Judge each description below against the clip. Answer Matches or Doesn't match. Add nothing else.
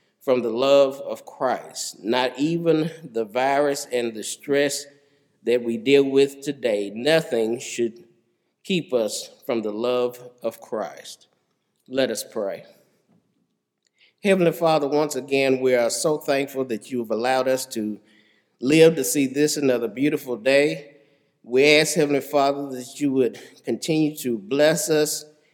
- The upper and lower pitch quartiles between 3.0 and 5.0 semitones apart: Matches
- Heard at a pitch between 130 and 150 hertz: Matches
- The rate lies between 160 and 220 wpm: Doesn't match